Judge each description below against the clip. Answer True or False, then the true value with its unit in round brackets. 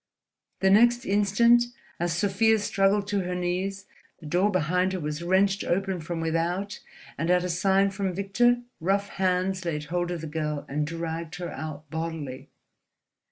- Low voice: False (180 Hz)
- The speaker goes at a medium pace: True (160 wpm)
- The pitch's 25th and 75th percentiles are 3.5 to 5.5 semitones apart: False (3.1 semitones)